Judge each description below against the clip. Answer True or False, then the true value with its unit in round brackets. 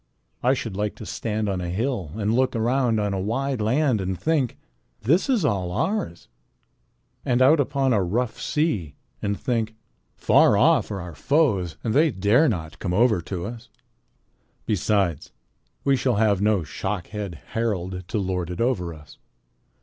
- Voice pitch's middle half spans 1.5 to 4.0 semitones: False (5.4 semitones)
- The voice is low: True (105 Hz)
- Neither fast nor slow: True (165 wpm)